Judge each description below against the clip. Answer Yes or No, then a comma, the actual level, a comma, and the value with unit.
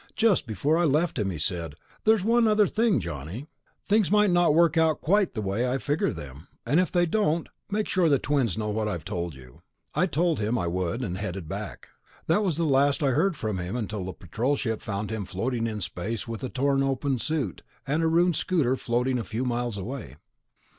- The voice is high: No, low, 130 Hz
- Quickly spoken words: Yes, fast, 215 wpm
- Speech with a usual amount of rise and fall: No, wide, 8.0 semitones